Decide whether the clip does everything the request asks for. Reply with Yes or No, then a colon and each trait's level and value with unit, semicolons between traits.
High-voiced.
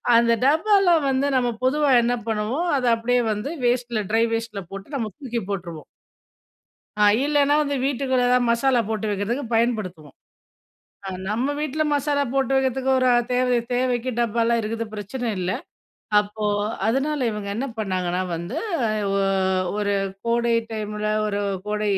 Yes: high, 235 Hz